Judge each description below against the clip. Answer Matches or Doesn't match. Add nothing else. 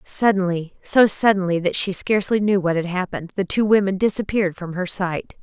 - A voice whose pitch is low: Doesn't match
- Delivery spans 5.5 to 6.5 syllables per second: Matches